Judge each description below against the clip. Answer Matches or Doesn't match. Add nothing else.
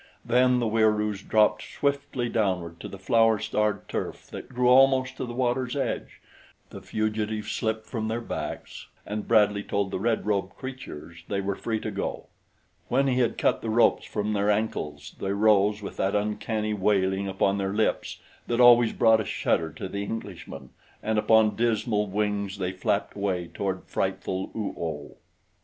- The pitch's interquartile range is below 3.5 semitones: Matches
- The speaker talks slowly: Doesn't match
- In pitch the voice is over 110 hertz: Doesn't match